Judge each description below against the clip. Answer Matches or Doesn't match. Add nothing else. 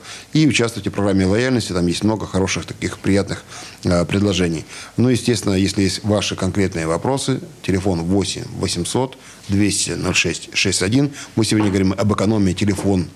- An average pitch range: Matches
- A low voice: Matches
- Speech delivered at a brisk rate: Doesn't match